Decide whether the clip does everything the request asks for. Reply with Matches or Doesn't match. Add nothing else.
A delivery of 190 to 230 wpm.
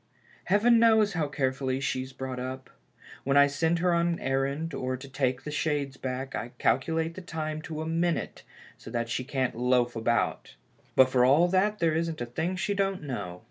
Matches